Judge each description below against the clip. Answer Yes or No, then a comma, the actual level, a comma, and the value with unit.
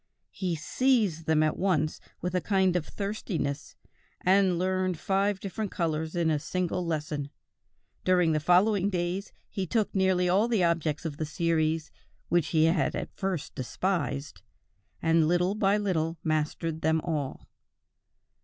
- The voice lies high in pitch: No, medium, 175 Hz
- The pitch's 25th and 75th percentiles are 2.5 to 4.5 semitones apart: Yes, average, 3.3 semitones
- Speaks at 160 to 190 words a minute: No, average, 145 wpm